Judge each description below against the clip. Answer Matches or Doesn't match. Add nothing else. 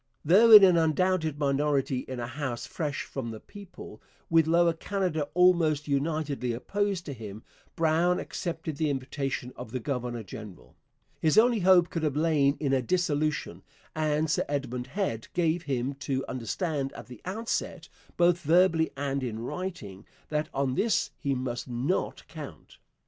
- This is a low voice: Doesn't match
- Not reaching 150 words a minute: Doesn't match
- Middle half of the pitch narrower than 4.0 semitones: Doesn't match